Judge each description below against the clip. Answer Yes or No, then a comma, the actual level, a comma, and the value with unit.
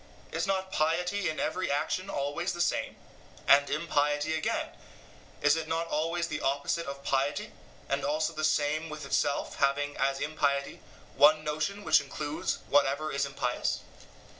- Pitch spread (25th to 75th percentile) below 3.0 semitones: Yes, narrow, 2.4 semitones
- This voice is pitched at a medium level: Yes, medium, 150 Hz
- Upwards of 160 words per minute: No, average, 150 wpm